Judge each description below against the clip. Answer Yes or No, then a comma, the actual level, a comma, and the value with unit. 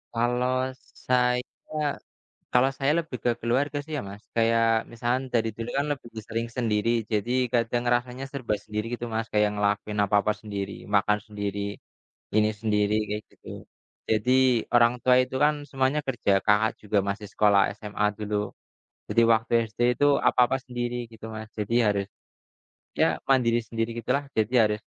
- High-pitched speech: No, low, 115 Hz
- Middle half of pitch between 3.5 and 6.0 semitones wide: No, average, 2.9 semitones